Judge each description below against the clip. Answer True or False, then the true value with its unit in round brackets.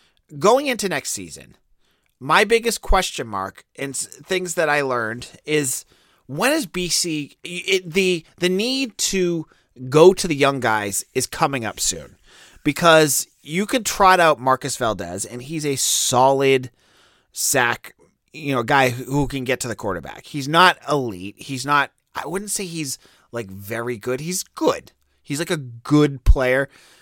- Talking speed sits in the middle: True (160 wpm)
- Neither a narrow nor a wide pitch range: False (5.9 semitones)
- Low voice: False (145 Hz)